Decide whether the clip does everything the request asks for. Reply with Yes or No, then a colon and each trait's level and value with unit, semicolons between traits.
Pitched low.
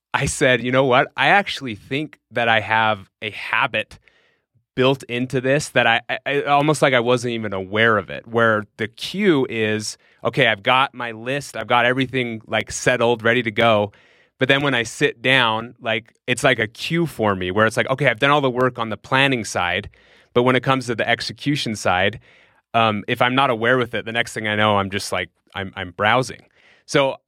Yes: low, 120 Hz